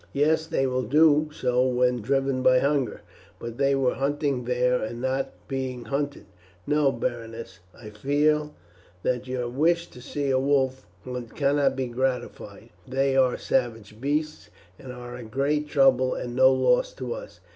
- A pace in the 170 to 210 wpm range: No, average, 155 wpm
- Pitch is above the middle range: No, low, 130 Hz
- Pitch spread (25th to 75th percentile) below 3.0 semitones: Yes, narrow, 2.5 semitones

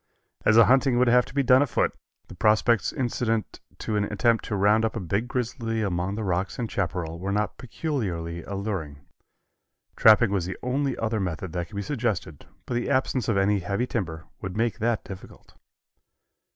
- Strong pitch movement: No, average, 4.1 semitones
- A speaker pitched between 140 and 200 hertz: No, low, 110 Hz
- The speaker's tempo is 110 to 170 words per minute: No, average, 185 wpm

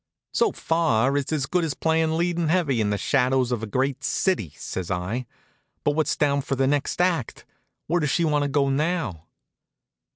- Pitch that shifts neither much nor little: Yes, average, 4.3 semitones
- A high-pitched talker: No, medium, 140 Hz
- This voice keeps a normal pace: Yes, average, 190 wpm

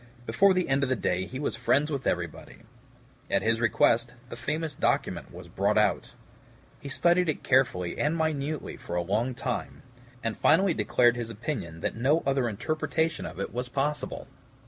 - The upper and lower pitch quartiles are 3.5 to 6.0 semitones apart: Yes, average, 5.1 semitones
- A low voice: Yes, low, 130 Hz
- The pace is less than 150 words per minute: No, average, 175 wpm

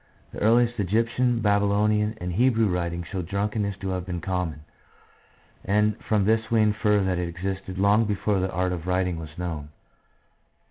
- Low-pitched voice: Yes, low, 100 Hz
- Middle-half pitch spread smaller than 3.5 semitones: Yes, average, 3.0 semitones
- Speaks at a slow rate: No, average, 160 wpm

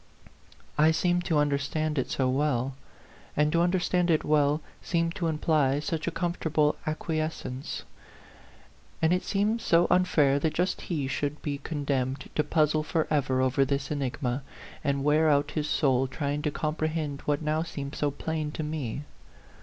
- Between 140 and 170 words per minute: Yes, average, 155 wpm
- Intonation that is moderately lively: No, narrow, 2.2 semitones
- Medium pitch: Yes, medium, 150 Hz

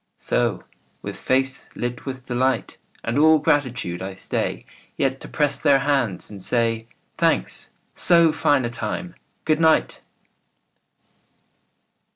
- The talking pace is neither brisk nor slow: No, slow, 125 wpm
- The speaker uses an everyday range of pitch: Yes, average, 4.0 semitones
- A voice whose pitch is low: Yes, low, 130 Hz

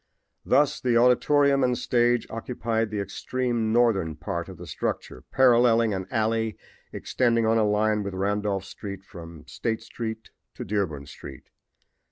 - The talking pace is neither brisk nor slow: Yes, average, 145 wpm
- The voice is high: No, low, 110 Hz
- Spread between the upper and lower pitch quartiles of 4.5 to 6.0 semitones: No, average, 3.4 semitones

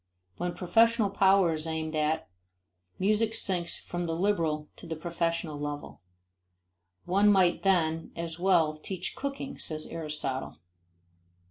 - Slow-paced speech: Yes, slow, 125 wpm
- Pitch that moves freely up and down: No, average, 3.5 semitones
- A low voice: No, medium, 170 Hz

